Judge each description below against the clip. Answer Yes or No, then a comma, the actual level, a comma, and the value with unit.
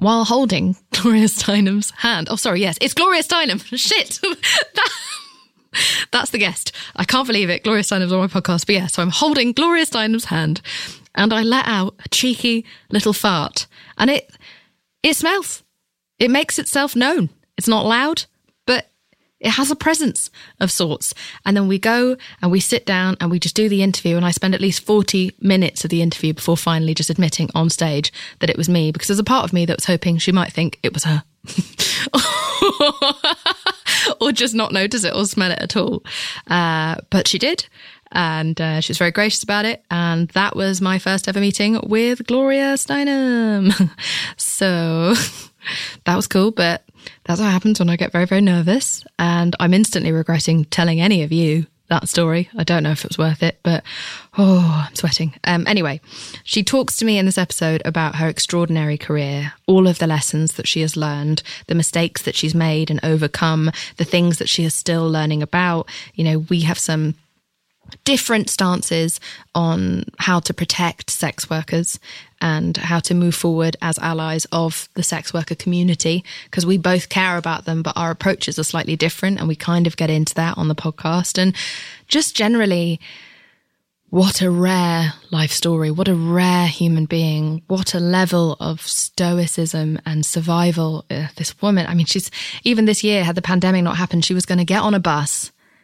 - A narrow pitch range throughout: No, average, 4.1 semitones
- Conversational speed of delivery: Yes, average, 185 wpm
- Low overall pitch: No, medium, 175 Hz